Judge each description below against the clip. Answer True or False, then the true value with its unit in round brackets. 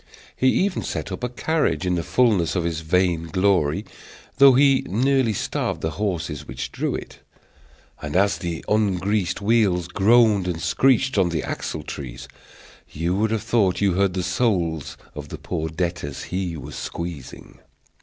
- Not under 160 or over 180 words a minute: True (165 wpm)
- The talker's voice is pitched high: False (95 Hz)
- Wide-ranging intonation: False (4.8 semitones)